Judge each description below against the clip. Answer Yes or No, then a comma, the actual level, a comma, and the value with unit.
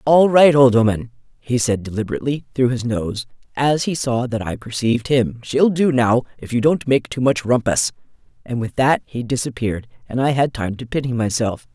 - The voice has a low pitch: Yes, low, 125 Hz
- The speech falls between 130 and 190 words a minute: No, average, 200 wpm